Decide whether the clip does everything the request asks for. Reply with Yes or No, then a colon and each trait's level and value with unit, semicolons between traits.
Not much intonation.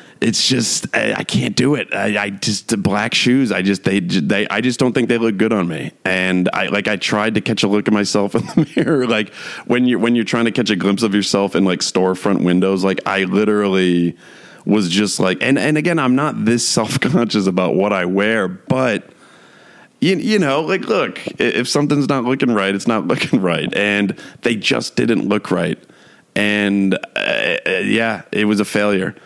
No: average, 3.2 semitones